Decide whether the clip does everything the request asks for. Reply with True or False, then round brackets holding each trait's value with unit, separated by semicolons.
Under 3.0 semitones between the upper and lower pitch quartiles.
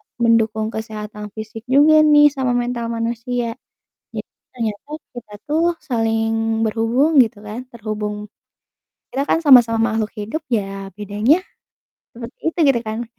True (2.6 semitones)